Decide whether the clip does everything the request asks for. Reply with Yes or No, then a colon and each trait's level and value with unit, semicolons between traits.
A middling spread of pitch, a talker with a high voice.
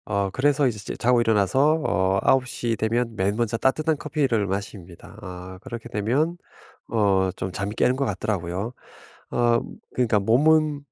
No: average, 4.9 semitones; low, 115 Hz